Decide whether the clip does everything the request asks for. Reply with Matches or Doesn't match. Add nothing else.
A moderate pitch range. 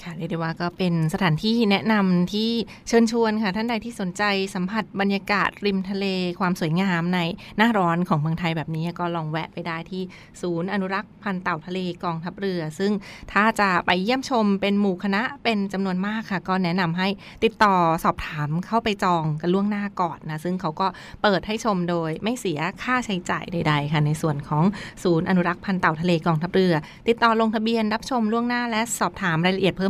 Matches